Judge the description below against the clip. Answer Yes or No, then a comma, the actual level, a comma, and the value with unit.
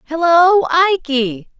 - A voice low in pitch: No, very high, 315 Hz